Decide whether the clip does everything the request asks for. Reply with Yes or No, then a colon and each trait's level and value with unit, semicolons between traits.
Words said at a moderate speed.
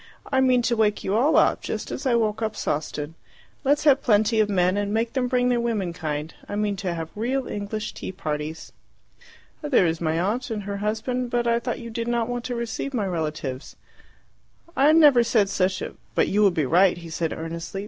No: fast, 215 wpm